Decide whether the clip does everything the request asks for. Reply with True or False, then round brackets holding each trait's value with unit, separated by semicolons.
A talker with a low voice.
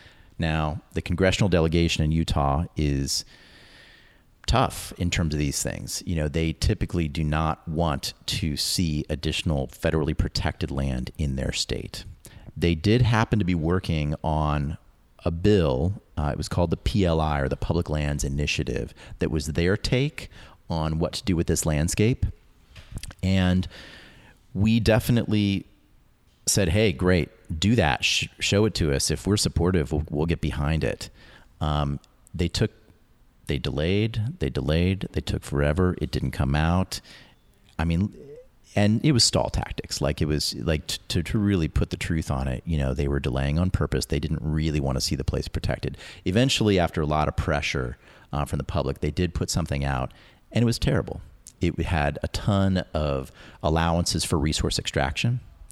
True (85 Hz)